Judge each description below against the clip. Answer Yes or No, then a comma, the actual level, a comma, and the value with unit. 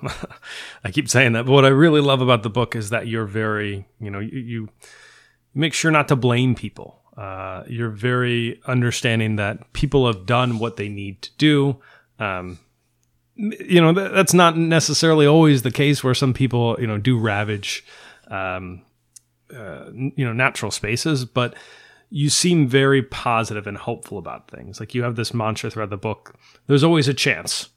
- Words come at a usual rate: Yes, average, 180 wpm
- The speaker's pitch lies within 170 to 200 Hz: No, low, 120 Hz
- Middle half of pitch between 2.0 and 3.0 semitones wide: No, average, 4.7 semitones